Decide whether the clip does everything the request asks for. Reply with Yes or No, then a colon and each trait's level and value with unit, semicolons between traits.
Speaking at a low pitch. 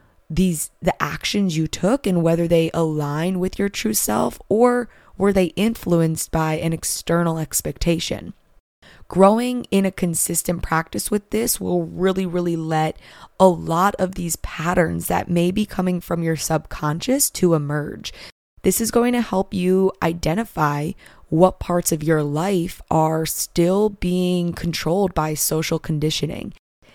No: medium, 175 Hz